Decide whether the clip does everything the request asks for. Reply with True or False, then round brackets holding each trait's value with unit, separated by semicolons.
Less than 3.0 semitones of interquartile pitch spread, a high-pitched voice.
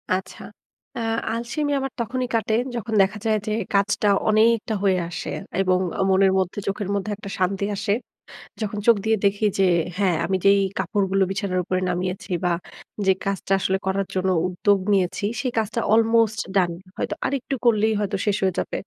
True (2.5 semitones; 200 Hz)